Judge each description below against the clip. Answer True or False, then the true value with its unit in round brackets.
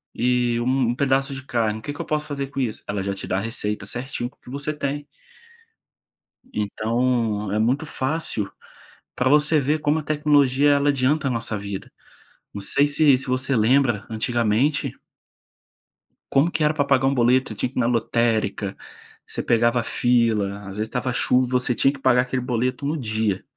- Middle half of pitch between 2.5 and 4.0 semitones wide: True (3.7 semitones)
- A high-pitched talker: False (125 Hz)